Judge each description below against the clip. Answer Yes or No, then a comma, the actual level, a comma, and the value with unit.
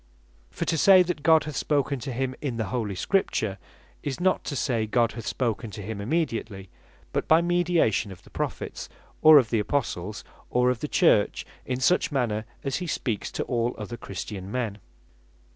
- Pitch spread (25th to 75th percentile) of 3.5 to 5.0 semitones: No, wide, 5.4 semitones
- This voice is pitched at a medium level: No, low, 125 Hz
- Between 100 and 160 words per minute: No, average, 185 wpm